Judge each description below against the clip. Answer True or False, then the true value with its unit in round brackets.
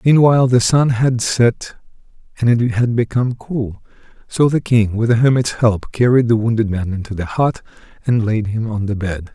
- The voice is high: False (115 Hz)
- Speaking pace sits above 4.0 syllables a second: True (5.0 syllables/s)